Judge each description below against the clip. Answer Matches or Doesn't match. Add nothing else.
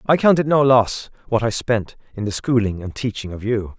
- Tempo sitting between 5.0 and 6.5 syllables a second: Matches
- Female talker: Doesn't match